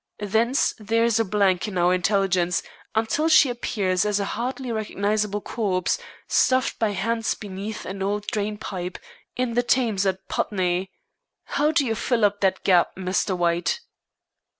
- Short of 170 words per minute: Yes, average, 155 wpm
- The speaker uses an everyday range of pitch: Yes, average, 3.2 semitones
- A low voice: No, high, 205 Hz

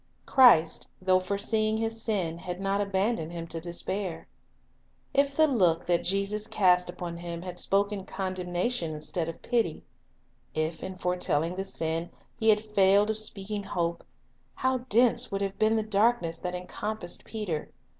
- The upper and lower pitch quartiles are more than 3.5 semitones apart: Yes, average, 3.9 semitones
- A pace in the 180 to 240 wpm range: No, average, 155 wpm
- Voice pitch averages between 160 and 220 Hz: Yes, high, 190 Hz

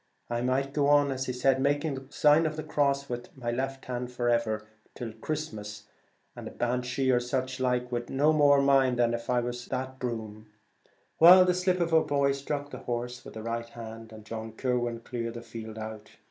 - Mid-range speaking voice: No, low, 125 Hz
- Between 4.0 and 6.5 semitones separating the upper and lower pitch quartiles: No, average, 3.0 semitones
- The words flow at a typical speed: Yes, average, 195 wpm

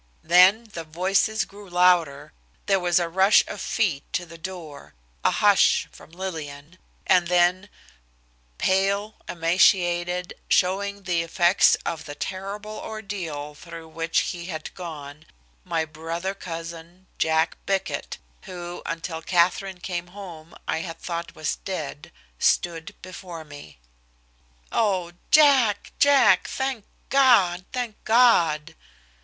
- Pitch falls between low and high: Yes, medium, 175 Hz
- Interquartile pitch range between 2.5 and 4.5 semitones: Yes, average, 3.0 semitones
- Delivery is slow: Yes, slow, 120 wpm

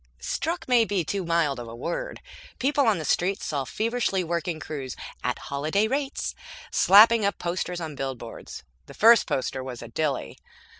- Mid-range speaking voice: Yes, medium, 170 Hz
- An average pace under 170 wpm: Yes, average, 160 wpm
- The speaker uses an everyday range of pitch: No, wide, 7.7 semitones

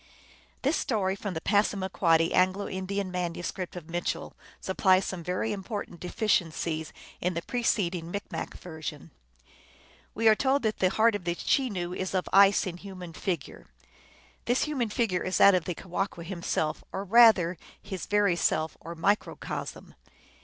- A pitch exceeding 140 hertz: Yes, medium, 185 Hz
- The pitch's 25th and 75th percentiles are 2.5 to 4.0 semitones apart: Yes, average, 2.8 semitones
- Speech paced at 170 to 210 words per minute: No, average, 155 wpm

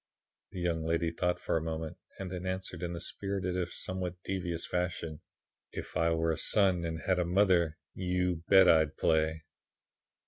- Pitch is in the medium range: No, very low, 85 Hz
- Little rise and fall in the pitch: Yes, narrow, 2.1 semitones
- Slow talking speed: No, average, 175 wpm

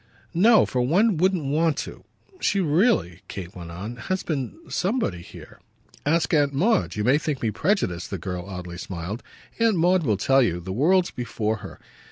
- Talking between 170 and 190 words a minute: Yes, average, 180 wpm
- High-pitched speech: No, low, 135 Hz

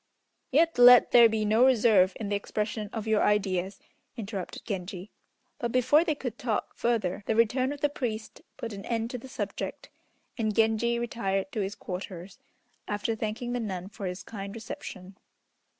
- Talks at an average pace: Yes, average, 170 wpm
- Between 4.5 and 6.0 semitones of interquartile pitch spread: No, average, 3.2 semitones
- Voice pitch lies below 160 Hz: No, high, 220 Hz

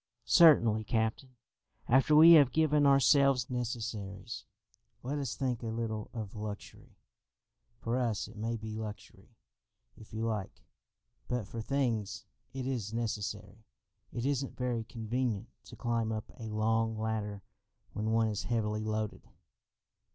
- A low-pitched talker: Yes, low, 115 Hz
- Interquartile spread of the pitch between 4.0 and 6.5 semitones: No, average, 2.7 semitones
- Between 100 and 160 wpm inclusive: Yes, slow, 135 wpm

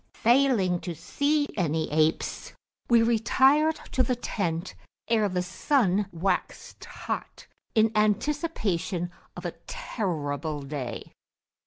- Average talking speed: No, slow, 110 wpm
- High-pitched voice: Yes, high, 200 Hz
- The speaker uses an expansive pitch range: Yes, wide, 6.9 semitones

